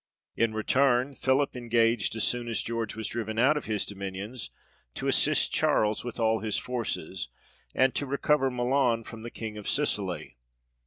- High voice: No, low, 115 Hz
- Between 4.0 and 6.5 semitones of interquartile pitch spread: No, average, 2.9 semitones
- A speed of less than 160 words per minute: No, average, 165 wpm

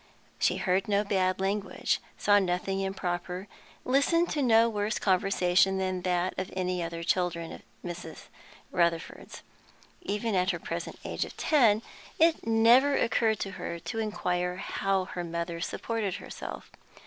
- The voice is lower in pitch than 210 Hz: Yes, high, 190 Hz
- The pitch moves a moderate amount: Yes, average, 3.3 semitones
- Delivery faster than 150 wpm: No, average, 145 wpm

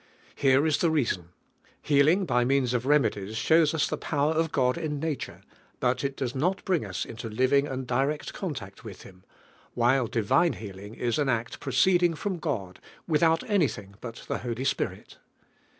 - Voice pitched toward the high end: No, low, 135 Hz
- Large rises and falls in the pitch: No, average, 4.9 semitones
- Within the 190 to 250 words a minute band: No, average, 175 wpm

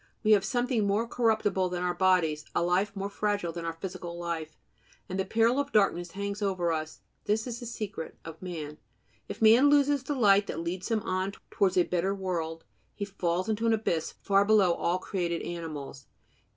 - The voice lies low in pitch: No, high, 190 Hz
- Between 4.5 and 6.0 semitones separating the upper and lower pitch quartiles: No, average, 3.8 semitones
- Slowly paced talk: No, average, 190 wpm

